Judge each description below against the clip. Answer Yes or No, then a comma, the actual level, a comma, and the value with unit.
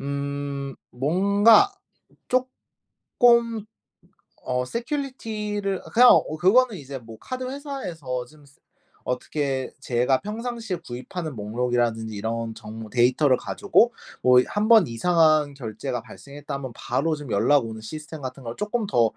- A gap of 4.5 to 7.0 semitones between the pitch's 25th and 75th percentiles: No, wide, 8.9 semitones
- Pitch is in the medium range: Yes, medium, 145 Hz